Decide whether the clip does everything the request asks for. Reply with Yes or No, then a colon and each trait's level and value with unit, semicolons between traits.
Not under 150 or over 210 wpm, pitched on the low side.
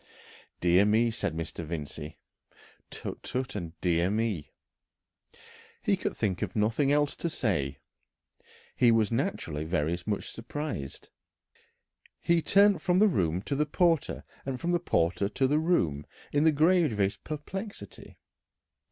No: average, 140 wpm; low, 115 Hz